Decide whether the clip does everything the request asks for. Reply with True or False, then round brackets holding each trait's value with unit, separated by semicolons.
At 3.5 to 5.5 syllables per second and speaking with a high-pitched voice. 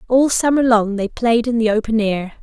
True (5.0 syllables/s; 230 Hz)